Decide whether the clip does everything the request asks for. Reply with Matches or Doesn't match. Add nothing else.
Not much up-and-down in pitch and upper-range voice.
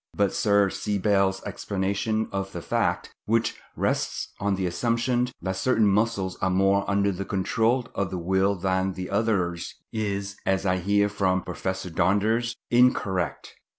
Doesn't match